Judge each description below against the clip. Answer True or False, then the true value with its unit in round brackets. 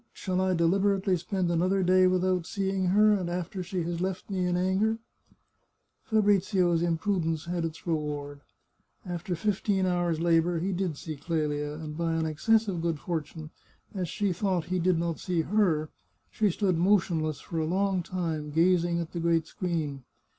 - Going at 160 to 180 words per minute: True (170 wpm)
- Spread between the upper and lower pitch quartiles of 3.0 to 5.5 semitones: False (2.5 semitones)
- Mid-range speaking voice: True (175 Hz)